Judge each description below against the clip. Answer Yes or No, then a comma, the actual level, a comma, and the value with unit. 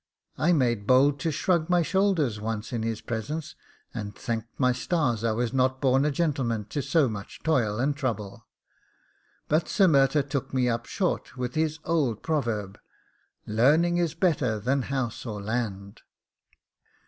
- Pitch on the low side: Yes, low, 130 Hz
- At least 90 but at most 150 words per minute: No, average, 160 wpm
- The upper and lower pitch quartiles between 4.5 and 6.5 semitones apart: Yes, average, 5.2 semitones